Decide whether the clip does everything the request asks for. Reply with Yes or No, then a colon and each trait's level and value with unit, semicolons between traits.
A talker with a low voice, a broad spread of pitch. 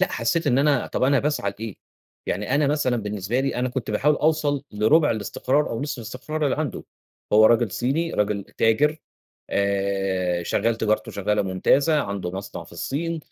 Yes: low, 120 Hz; wide, 6.1 semitones